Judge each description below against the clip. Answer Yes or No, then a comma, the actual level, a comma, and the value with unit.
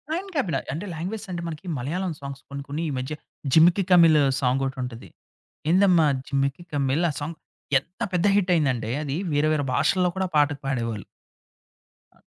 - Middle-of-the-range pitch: Yes, medium, 155 Hz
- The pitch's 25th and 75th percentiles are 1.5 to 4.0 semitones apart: No, average, 4.4 semitones